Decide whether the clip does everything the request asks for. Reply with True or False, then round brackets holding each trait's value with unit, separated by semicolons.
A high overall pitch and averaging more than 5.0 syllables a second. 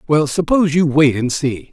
False (145 Hz; 5.2 syllables/s)